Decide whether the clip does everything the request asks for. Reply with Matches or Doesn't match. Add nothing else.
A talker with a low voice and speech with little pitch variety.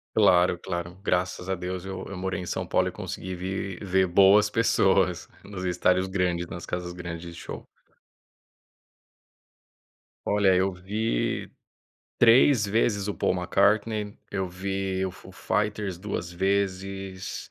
Matches